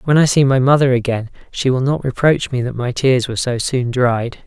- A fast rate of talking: Yes, fast, 240 wpm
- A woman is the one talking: No, male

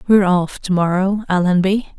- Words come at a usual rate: Yes, average, 150 wpm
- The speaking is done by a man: No, female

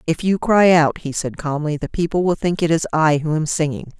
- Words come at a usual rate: No, fast, 255 wpm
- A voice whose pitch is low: No, medium, 160 Hz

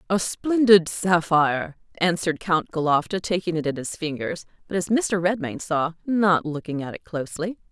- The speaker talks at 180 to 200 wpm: No, average, 165 wpm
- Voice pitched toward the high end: No, medium, 175 Hz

